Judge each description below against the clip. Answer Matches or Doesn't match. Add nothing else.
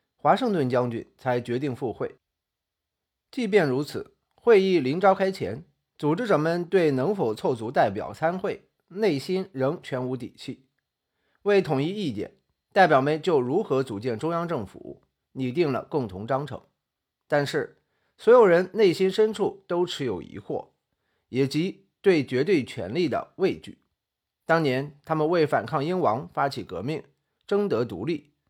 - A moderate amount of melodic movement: Doesn't match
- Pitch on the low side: Doesn't match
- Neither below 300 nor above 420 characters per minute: Doesn't match